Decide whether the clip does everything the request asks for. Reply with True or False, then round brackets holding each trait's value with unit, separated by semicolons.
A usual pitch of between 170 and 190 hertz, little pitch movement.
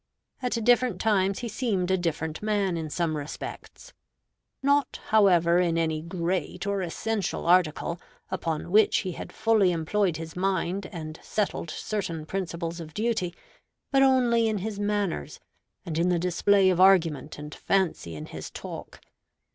False (185 Hz; 3.9 semitones)